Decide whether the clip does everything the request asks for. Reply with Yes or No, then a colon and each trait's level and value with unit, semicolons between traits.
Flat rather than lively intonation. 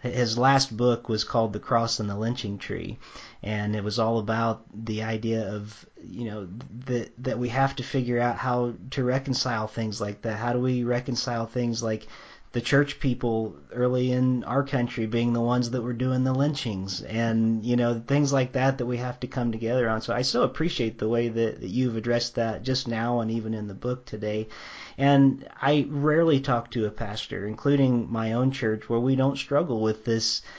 Yes: narrow, 2.3 semitones